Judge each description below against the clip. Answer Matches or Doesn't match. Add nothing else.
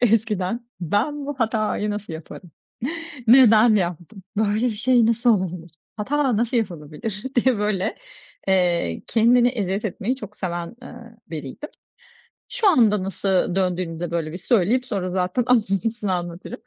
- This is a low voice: Doesn't match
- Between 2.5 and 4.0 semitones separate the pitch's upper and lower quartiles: Doesn't match